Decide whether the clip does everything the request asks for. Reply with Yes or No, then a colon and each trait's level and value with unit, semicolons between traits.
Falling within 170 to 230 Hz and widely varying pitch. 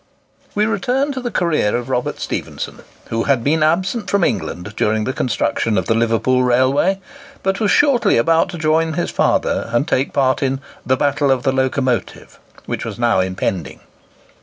No: low, 135 Hz; wide, 6.5 semitones